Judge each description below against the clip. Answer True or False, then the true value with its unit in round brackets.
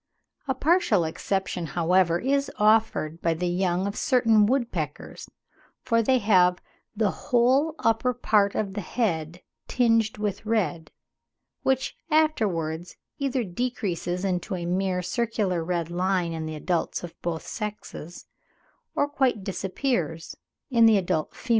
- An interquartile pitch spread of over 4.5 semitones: True (5.1 semitones)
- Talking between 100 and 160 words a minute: True (135 wpm)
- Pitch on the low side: False (195 Hz)